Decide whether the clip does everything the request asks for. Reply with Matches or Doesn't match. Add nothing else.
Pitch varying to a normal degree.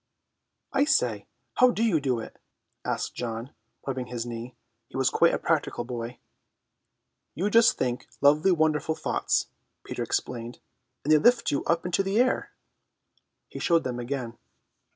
Doesn't match